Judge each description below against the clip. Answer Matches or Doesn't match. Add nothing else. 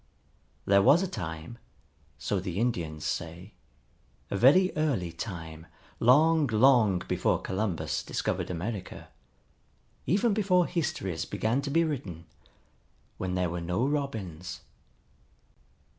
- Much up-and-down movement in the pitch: Matches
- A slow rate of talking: Matches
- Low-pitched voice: Matches